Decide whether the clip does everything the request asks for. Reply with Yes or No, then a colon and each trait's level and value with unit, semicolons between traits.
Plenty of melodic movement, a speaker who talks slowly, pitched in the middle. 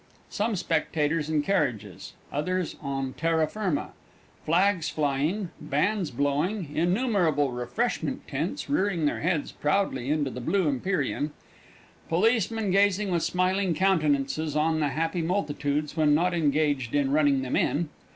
No: average, 4.3 semitones; slow, 130 wpm; medium, 160 Hz